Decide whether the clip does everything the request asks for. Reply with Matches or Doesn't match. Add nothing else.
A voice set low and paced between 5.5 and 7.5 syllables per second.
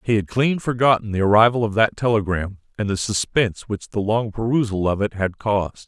Matches